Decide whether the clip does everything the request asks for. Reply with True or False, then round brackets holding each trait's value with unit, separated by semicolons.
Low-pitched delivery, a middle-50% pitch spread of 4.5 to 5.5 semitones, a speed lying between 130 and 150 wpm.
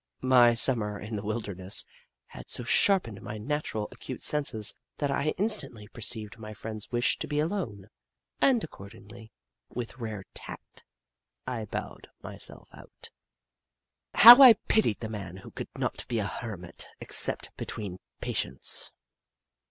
True (110 Hz; 5.1 semitones; 140 wpm)